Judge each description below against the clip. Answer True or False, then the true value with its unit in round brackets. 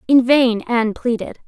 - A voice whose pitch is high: True (245 Hz)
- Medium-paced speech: True (165 wpm)